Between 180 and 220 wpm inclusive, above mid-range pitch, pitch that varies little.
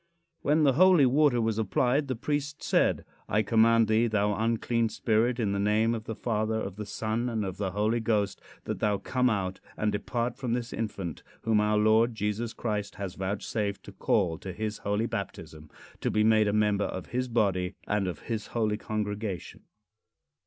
No: average, 190 wpm; low, 110 Hz; narrow, 2.3 semitones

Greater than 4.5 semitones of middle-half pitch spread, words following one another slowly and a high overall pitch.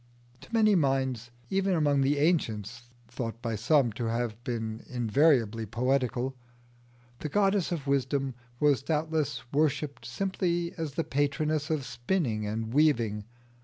No: average, 4.9 semitones; slow, 130 wpm; low, 135 Hz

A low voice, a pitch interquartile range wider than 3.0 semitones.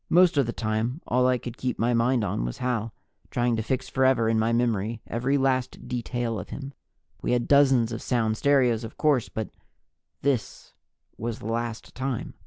No: low, 120 Hz; narrow, 2.5 semitones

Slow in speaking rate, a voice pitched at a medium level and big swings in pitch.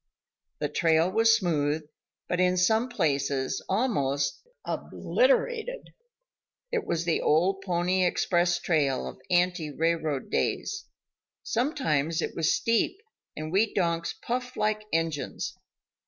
Yes: slow, 115 wpm; medium, 175 Hz; wide, 5.9 semitones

